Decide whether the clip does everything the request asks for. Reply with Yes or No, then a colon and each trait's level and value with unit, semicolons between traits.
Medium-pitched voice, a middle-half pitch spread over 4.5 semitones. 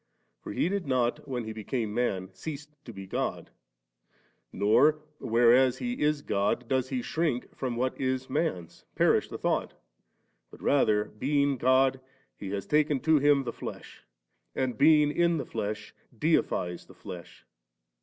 No: low, 130 Hz; average, 5.0 semitones